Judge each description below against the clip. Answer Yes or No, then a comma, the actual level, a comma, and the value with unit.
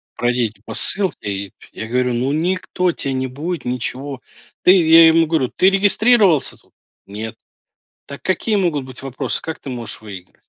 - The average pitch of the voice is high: No, medium, 140 Hz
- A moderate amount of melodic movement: No, wide, 6.1 semitones